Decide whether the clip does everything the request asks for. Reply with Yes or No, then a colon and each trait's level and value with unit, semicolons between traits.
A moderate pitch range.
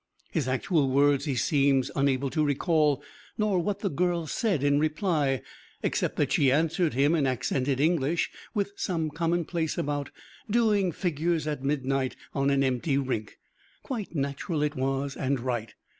Yes: average, 3.7 semitones